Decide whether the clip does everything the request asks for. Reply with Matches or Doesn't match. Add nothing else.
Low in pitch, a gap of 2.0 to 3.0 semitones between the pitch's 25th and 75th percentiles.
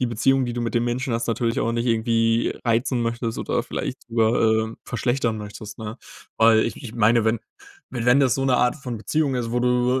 Doesn't match